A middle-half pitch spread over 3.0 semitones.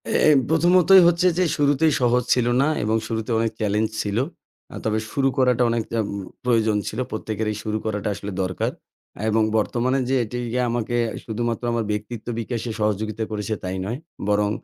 No: average, 2.7 semitones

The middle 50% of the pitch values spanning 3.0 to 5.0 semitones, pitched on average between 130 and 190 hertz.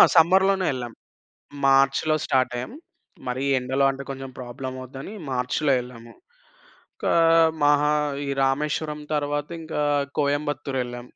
No: narrow, 2.6 semitones; low, 135 Hz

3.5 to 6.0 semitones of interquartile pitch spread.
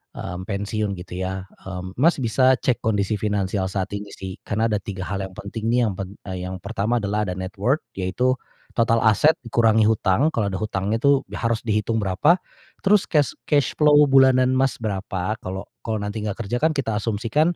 Yes: average, 4.1 semitones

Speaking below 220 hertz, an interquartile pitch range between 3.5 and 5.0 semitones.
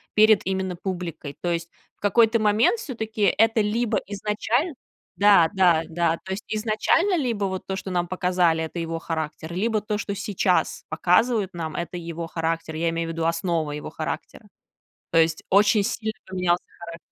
Yes: medium, 185 Hz; average, 4.2 semitones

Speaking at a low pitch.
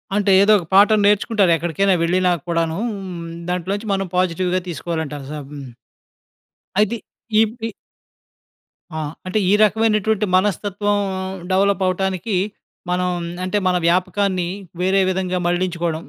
No: medium, 185 Hz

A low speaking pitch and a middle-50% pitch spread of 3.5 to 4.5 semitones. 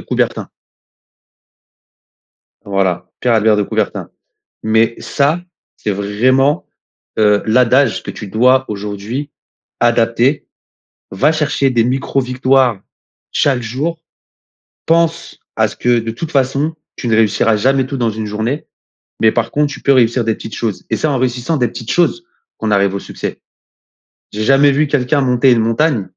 Yes: low, 125 Hz; average, 3.9 semitones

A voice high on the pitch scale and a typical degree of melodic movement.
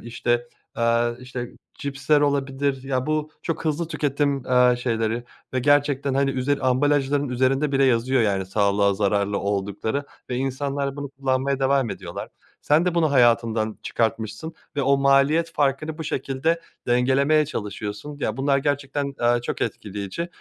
No: low, 135 Hz; average, 3.2 semitones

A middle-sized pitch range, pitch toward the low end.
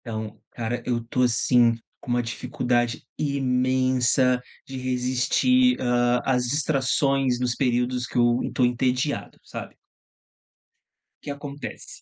No: narrow, 1.6 semitones; low, 125 Hz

